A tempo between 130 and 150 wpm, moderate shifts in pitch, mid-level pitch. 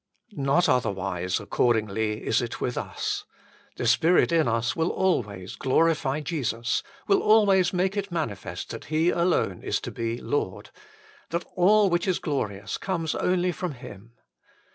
No: average, 145 wpm; wide, 7.9 semitones; medium, 150 Hz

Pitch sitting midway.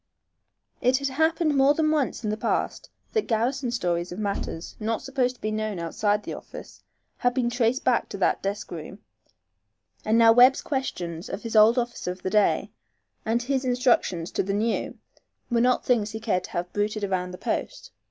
No: high, 225 Hz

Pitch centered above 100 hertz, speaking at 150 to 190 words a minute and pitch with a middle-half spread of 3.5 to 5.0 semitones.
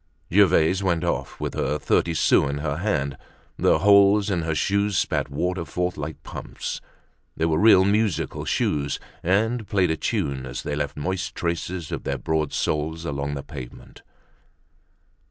No: very low, 85 Hz; average, 160 wpm; average, 4.6 semitones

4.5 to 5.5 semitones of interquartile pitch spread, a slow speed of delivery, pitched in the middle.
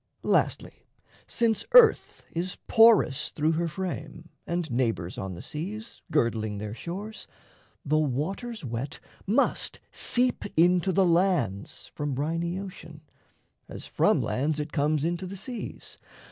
Yes: average, 5.2 semitones; slow, 130 wpm; medium, 165 Hz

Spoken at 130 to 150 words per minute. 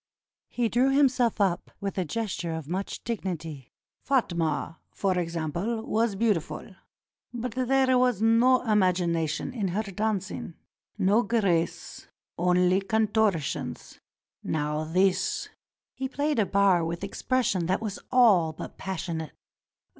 Yes: slow, 135 wpm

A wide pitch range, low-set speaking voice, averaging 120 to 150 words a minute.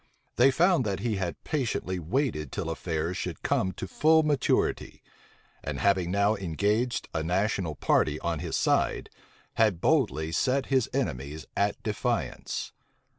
Yes: wide, 7.6 semitones; low, 100 Hz; average, 140 wpm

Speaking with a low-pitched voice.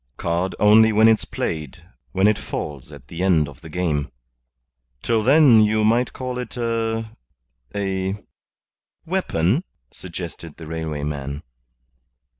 Yes: very low, 95 Hz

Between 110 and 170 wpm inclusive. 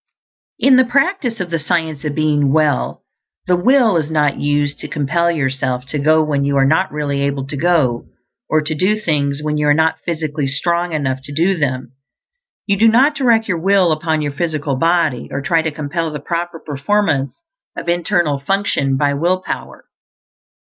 No: average, 185 wpm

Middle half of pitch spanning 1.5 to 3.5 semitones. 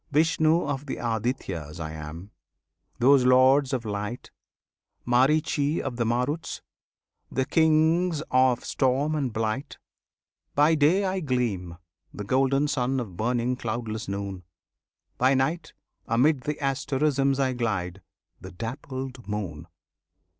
No: average, 4.5 semitones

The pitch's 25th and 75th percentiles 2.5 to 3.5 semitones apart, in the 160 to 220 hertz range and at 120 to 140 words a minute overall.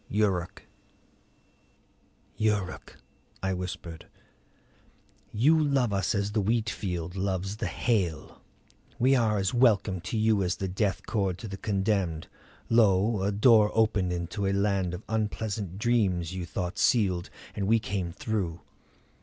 No: average, 3.1 semitones; low, 100 Hz; slow, 135 wpm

